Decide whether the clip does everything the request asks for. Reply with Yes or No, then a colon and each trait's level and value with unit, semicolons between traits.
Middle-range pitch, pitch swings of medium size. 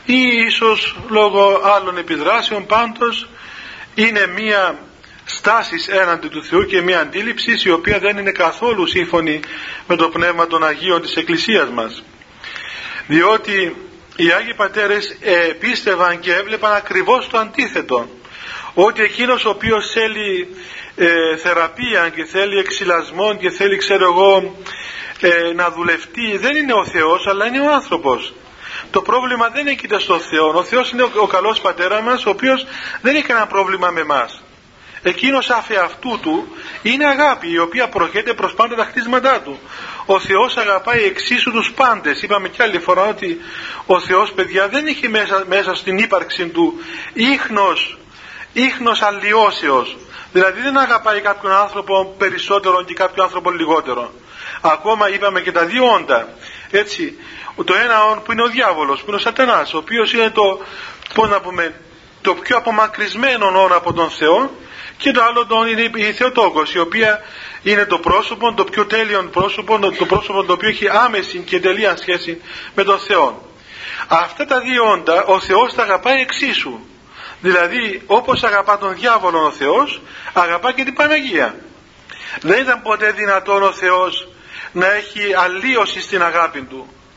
No: high, 205 Hz; average, 4.4 semitones